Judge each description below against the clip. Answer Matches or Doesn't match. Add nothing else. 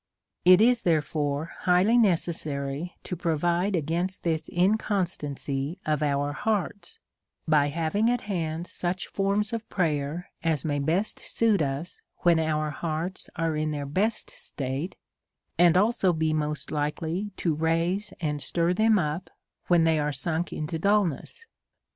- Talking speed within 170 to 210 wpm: Doesn't match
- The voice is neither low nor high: Matches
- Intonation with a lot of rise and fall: Doesn't match